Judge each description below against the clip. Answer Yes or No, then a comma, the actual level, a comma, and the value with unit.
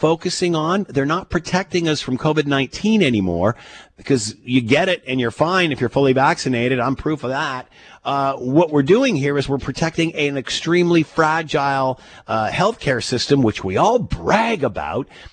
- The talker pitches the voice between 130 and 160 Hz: Yes, medium, 140 Hz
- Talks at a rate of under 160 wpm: No, average, 170 wpm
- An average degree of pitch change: Yes, average, 4.1 semitones